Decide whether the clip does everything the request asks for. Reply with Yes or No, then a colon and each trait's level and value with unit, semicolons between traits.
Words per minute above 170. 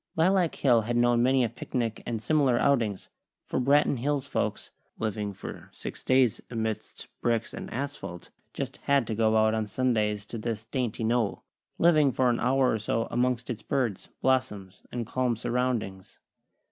No: average, 165 wpm